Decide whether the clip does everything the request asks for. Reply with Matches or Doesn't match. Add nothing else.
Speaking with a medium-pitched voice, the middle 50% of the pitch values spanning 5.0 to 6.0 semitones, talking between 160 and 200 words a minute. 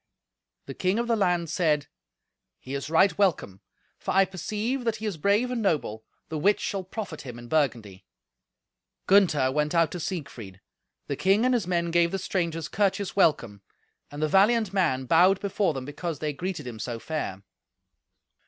Matches